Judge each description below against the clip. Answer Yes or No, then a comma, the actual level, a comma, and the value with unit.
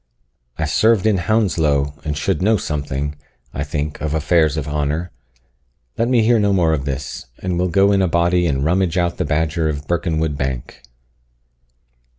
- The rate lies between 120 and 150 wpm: No, average, 170 wpm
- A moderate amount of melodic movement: Yes, average, 4.1 semitones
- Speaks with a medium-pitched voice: No, very low, 80 Hz